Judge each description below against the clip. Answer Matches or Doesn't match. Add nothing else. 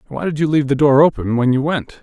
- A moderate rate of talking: Doesn't match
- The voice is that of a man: Matches